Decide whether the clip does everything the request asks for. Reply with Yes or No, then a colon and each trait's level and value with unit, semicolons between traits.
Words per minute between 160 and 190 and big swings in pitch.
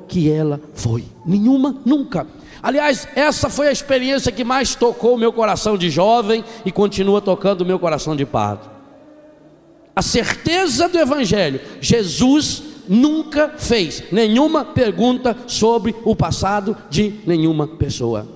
No: average, 135 wpm; wide, 7.6 semitones